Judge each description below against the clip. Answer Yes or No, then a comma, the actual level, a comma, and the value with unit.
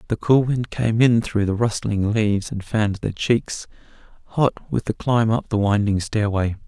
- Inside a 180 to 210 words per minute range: Yes, average, 200 wpm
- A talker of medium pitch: No, low, 110 Hz